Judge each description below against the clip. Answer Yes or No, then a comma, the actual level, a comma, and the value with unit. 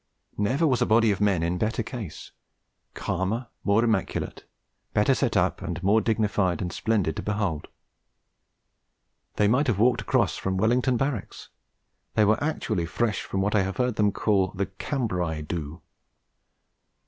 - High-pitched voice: No, low, 105 Hz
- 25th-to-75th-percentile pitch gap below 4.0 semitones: Yes, average, 3.6 semitones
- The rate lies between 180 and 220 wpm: No, average, 150 wpm